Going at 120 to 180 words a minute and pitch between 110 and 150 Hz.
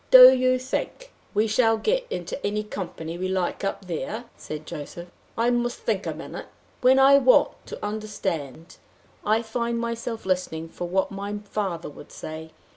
No: average, 165 wpm; high, 210 Hz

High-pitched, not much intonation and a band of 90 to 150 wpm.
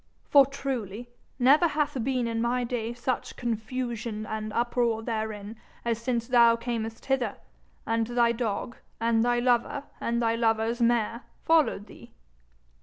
Yes: high, 235 Hz; narrow, 1.6 semitones; average, 140 wpm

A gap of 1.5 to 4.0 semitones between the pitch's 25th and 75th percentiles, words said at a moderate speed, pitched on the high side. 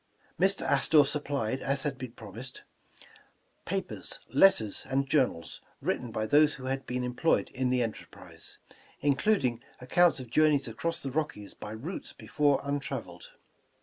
No: average, 3.2 semitones; average, 150 wpm; low, 135 Hz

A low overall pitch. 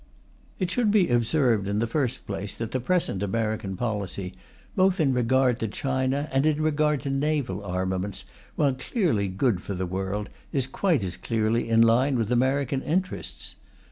Yes: low, 120 Hz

